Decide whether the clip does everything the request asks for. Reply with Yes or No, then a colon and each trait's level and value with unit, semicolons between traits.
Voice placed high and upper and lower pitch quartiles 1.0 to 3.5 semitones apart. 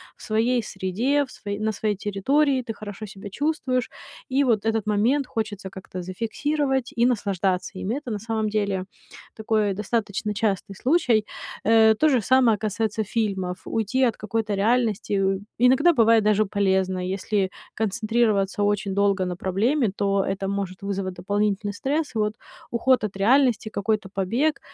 Yes: high, 215 Hz; average, 3.2 semitones